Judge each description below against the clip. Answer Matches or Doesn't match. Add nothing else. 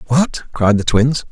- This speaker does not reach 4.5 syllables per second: Matches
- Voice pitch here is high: Doesn't match